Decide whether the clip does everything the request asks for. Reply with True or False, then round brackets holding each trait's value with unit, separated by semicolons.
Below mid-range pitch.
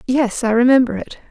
False (240 Hz)